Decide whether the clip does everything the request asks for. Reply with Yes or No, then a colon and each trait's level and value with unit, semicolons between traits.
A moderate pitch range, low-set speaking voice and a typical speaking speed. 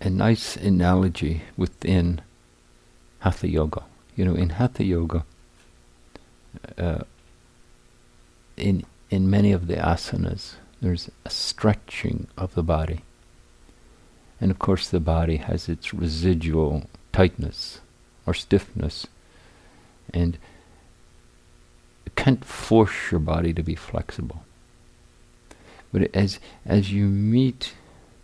No: average, 3.8 semitones; very low, 90 Hz; slow, 105 wpm